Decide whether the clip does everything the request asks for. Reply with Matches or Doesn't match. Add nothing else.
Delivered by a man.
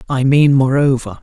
Matches